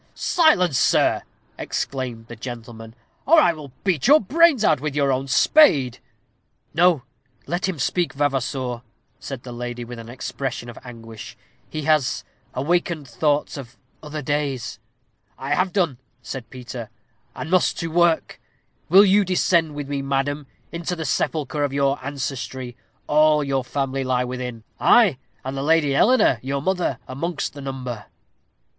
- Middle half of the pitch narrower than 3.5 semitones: No, average, 4.4 semitones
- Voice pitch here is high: No, medium, 140 Hz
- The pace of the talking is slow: No, average, 150 wpm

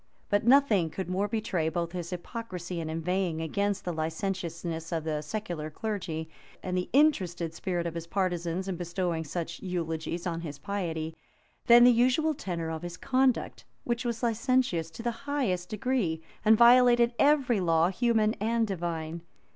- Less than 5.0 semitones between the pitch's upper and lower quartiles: No, wide, 5.6 semitones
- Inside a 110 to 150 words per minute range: No, average, 160 wpm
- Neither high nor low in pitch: Yes, medium, 180 Hz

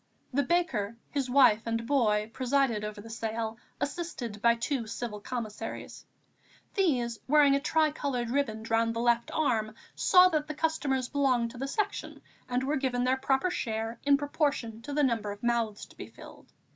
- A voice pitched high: Yes, high, 245 Hz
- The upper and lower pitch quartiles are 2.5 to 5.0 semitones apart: Yes, average, 3.9 semitones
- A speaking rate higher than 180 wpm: No, average, 170 wpm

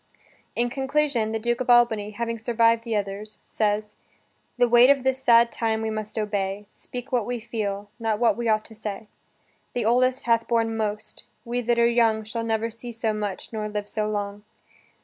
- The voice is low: No, high, 225 Hz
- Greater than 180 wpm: Yes, average, 190 wpm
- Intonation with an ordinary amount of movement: No, narrow, 2.0 semitones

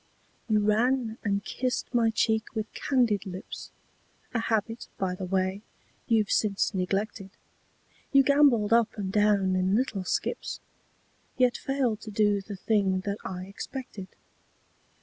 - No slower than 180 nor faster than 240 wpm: No, slow, 135 wpm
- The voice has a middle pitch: No, high, 210 Hz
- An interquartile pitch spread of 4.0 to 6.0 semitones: No, average, 3.0 semitones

